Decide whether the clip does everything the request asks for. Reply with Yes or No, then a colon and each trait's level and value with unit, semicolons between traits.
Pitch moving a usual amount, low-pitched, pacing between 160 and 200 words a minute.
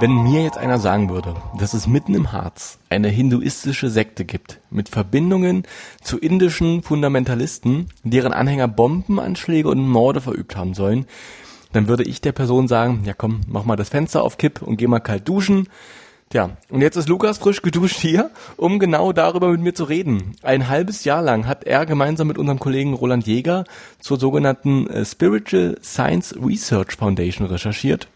No: wide, 6.7 semitones; low, 130 Hz; average, 175 wpm